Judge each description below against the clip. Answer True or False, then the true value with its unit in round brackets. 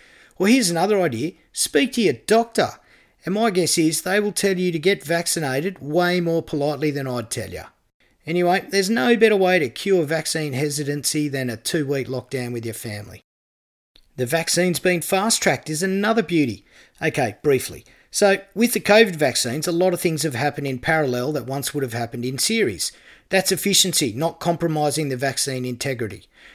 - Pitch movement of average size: False (5.9 semitones)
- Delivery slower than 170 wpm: False (180 wpm)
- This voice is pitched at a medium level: True (160 Hz)